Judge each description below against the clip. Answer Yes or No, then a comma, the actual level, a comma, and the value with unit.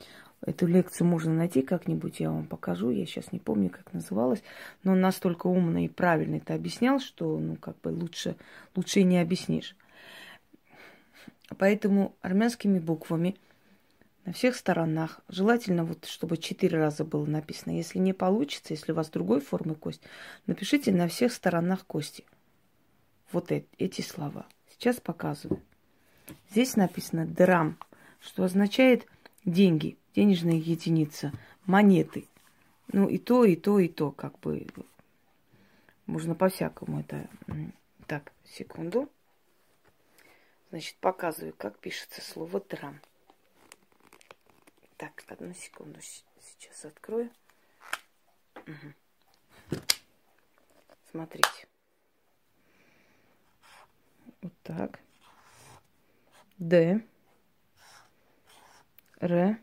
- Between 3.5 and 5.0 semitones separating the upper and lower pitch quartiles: Yes, average, 3.8 semitones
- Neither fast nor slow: No, slow, 105 wpm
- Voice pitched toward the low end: No, medium, 180 Hz